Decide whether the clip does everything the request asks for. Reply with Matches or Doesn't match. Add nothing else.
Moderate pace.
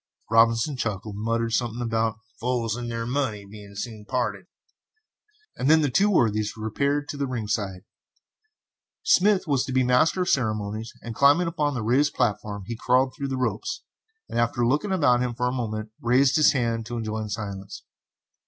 Matches